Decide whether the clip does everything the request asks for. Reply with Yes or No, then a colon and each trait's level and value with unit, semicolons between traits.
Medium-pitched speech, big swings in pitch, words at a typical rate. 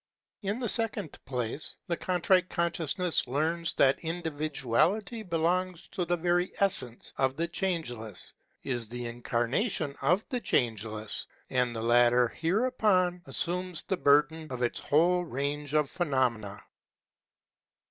No: medium, 160 Hz; wide, 6.3 semitones; slow, 125 wpm